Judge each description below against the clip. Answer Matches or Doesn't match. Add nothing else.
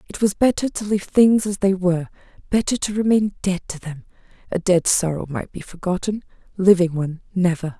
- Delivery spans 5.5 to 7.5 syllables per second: Matches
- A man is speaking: Doesn't match